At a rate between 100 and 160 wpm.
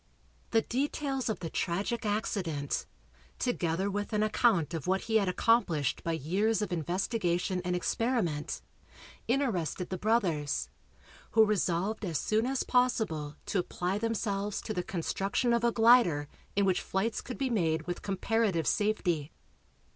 Yes: average, 145 wpm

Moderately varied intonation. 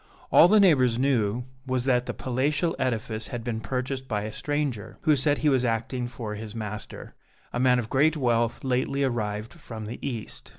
Yes: average, 3.3 semitones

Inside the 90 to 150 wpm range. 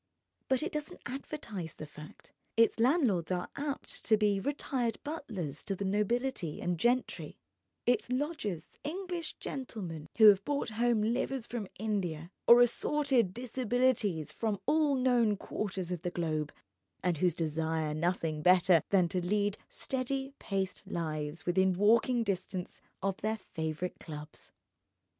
Yes: average, 140 wpm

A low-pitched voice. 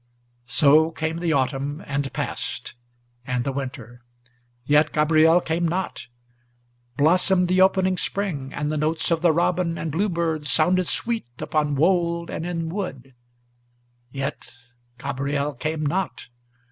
No: medium, 160 Hz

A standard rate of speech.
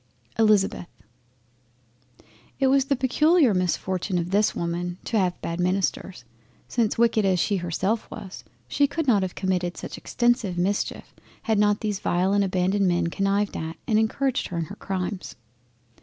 Yes: average, 155 wpm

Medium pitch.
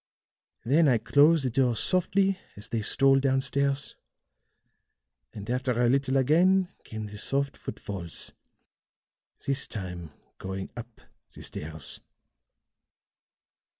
No: low, 130 Hz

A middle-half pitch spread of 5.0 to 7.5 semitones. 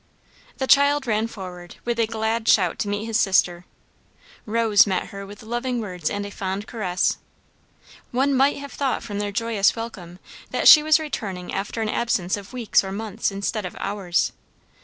No: average, 3.3 semitones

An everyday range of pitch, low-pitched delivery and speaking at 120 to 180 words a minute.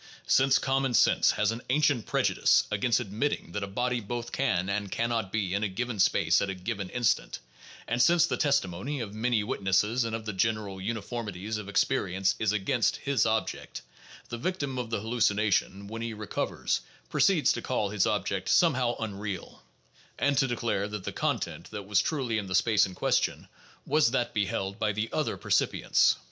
No: average, 3.4 semitones; low, 110 Hz; average, 190 wpm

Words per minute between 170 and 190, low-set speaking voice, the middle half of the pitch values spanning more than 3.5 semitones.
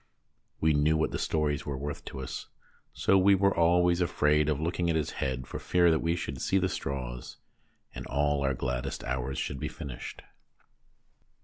Yes: average, 185 wpm; very low, 75 Hz; average, 4.1 semitones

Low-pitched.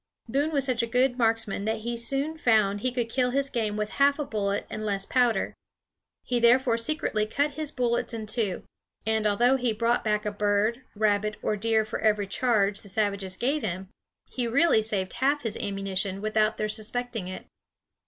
No: high, 225 Hz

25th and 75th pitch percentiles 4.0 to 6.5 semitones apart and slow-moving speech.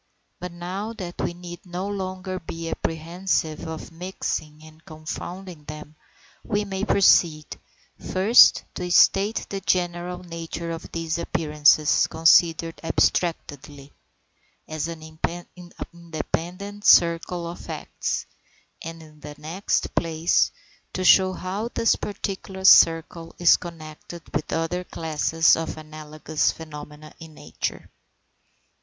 No: narrow, 2.6 semitones; slow, 115 wpm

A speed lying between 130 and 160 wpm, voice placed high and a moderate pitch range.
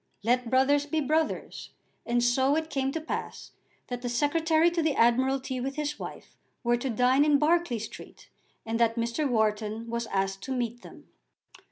No: average, 175 wpm; very high, 260 Hz; average, 4.0 semitones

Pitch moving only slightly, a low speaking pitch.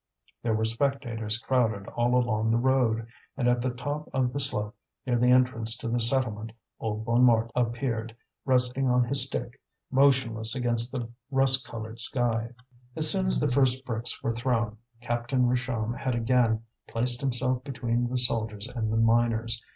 Yes: narrow, 2.1 semitones; low, 120 Hz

